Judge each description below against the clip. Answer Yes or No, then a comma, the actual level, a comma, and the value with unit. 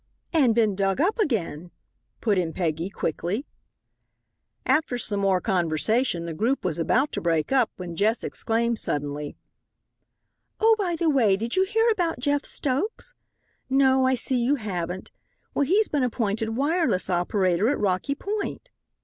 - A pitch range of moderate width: No, wide, 7.6 semitones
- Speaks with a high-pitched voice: Yes, high, 230 Hz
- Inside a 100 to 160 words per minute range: Yes, average, 150 wpm